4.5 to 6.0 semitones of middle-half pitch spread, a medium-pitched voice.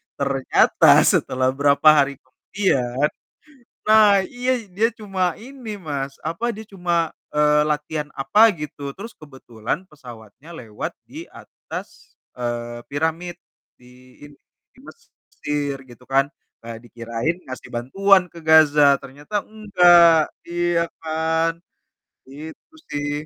Yes: average, 5.0 semitones; medium, 155 Hz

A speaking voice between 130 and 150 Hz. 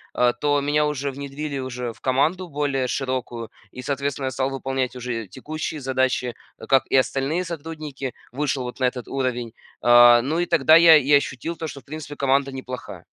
Yes: low, 135 Hz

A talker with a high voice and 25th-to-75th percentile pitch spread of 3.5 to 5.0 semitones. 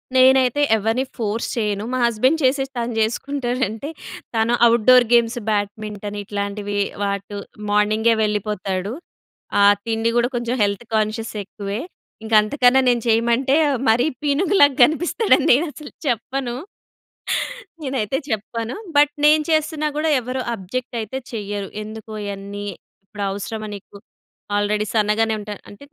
Yes: high, 225 Hz; average, 3.8 semitones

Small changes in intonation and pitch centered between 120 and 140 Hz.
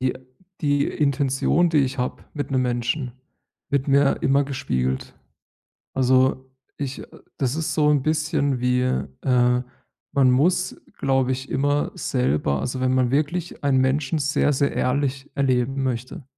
Yes: narrow, 2.1 semitones; low, 135 Hz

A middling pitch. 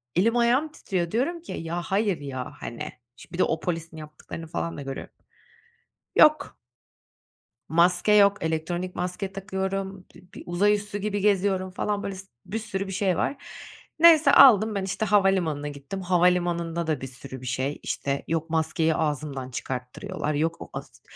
Yes: medium, 180 Hz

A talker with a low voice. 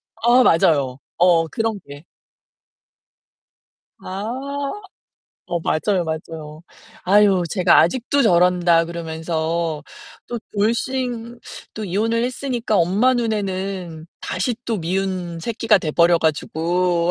No: medium, 185 Hz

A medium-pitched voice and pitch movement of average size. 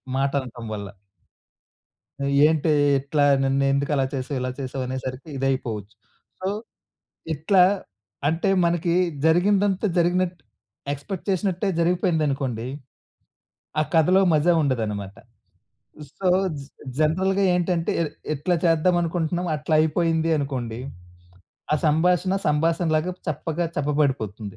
Yes: medium, 155 Hz; average, 4.6 semitones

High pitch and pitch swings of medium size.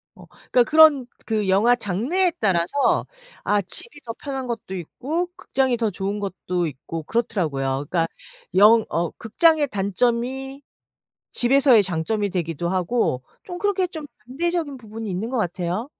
No: high, 225 Hz; wide, 6.6 semitones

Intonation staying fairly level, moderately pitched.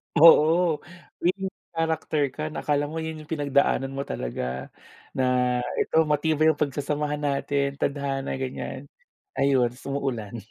Yes: narrow, 2.3 semitones; medium, 145 Hz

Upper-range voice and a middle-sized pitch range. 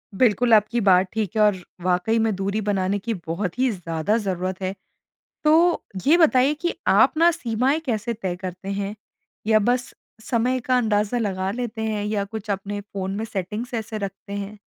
Yes: high, 210 Hz; average, 3.5 semitones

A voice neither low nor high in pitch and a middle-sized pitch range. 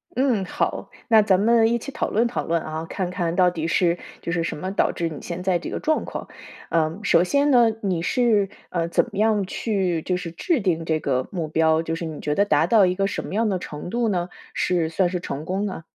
Yes: medium, 180 Hz; average, 4.0 semitones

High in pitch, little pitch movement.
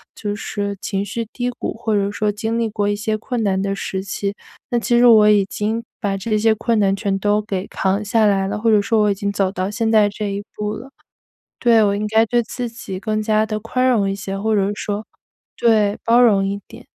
Yes: high, 210 Hz; narrow, 1.9 semitones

